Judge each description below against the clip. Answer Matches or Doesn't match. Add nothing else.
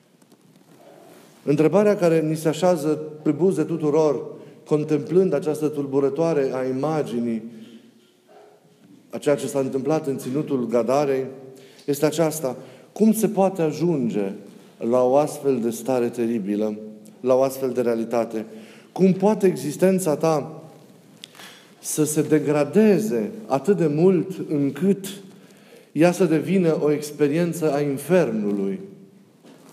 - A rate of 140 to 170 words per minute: Doesn't match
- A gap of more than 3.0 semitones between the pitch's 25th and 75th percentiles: Matches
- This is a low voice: Doesn't match